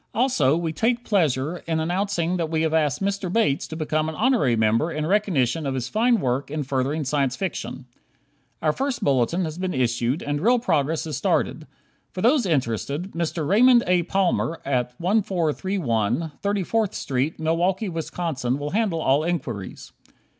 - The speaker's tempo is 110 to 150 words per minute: No, average, 160 wpm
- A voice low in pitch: No, medium, 160 Hz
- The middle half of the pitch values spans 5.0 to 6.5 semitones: Yes, wide, 5.5 semitones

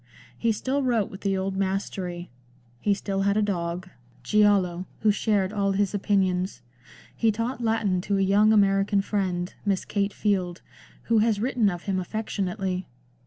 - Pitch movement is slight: Yes, narrow, 2.0 semitones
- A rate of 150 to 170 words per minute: Yes, average, 160 wpm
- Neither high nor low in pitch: No, high, 200 Hz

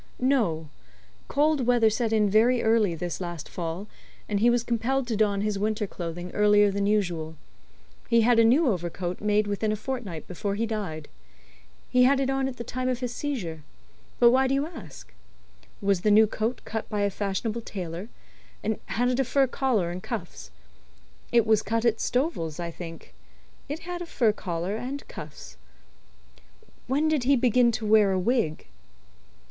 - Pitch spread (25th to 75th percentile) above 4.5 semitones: Yes, average, 4.9 semitones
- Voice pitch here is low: No, high, 215 Hz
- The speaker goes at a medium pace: Yes, average, 180 wpm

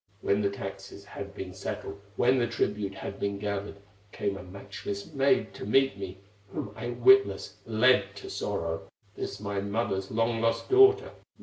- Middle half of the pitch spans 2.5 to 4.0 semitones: Yes, average, 3.0 semitones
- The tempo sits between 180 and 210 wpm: No, average, 165 wpm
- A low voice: Yes, low, 100 Hz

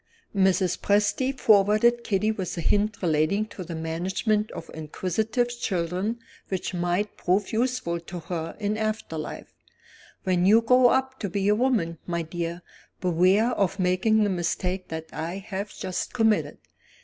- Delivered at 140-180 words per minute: Yes, average, 150 wpm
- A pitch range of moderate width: Yes, average, 3.8 semitones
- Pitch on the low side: No, high, 195 Hz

